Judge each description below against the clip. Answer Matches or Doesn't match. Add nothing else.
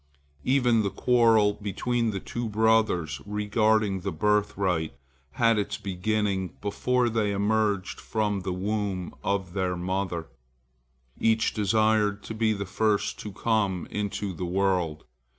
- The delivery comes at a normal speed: Doesn't match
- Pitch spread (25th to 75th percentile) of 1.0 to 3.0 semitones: Matches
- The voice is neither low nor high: Doesn't match